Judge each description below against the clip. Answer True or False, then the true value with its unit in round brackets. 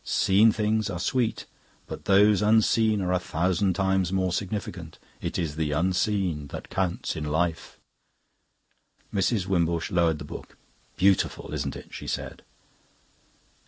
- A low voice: True (95 Hz)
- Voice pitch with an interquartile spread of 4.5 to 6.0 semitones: False (3.5 semitones)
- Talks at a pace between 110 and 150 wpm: True (135 wpm)